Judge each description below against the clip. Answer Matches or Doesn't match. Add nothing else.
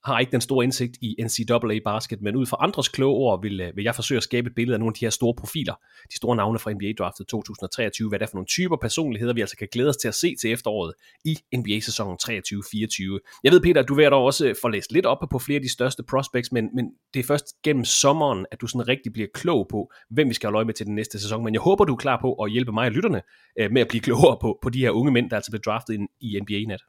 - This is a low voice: Matches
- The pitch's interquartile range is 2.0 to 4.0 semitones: Matches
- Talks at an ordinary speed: Doesn't match